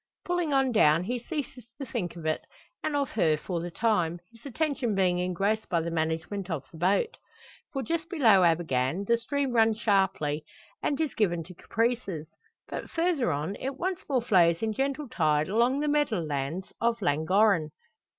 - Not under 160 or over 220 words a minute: Yes, average, 180 wpm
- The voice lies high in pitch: Yes, high, 210 Hz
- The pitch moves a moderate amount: No, wide, 7.5 semitones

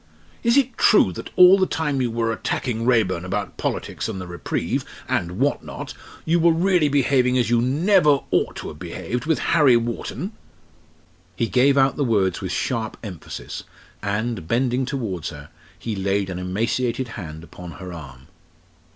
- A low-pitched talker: Yes, low, 120 Hz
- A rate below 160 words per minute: No, average, 170 wpm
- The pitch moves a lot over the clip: Yes, wide, 6.7 semitones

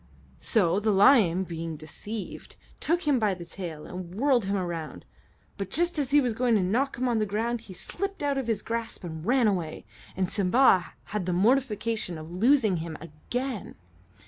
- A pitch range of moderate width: No, wide, 5.7 semitones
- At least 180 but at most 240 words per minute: Yes, average, 185 wpm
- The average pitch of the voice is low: No, high, 210 Hz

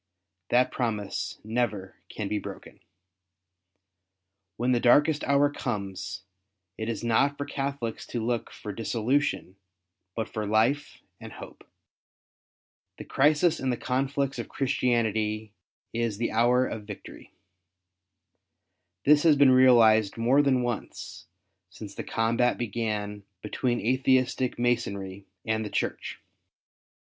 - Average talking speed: No, slow, 120 wpm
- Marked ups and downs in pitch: No, average, 3.2 semitones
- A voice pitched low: Yes, low, 120 Hz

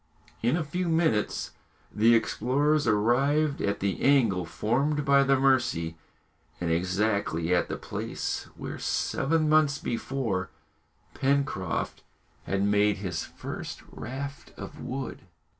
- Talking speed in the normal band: No, slow, 120 wpm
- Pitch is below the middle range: Yes, low, 125 Hz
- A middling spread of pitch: No, wide, 5.9 semitones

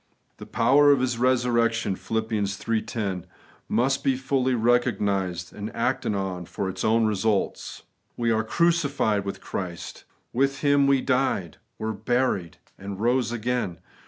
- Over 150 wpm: No, average, 140 wpm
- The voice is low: Yes, low, 115 Hz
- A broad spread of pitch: No, average, 4.3 semitones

